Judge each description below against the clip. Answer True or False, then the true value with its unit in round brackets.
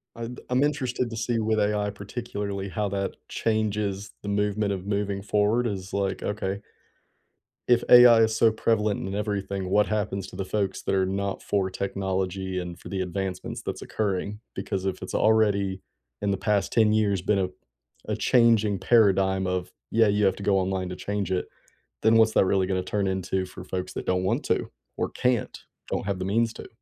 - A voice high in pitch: False (100 Hz)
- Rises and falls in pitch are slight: True (2.1 semitones)